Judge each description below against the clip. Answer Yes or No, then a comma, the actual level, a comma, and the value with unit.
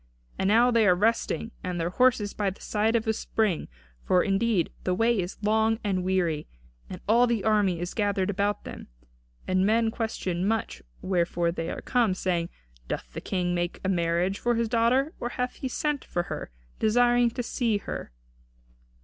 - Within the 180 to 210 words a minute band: Yes, average, 185 wpm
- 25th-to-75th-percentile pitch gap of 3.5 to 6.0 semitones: Yes, average, 4.1 semitones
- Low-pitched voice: No, high, 205 Hz